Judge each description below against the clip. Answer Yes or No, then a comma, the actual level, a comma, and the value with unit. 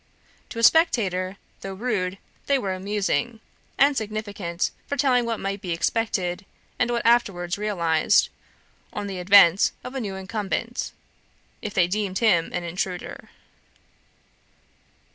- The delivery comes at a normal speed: No, slow, 130 wpm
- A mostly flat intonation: No, average, 4.0 semitones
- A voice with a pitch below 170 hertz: No, high, 200 Hz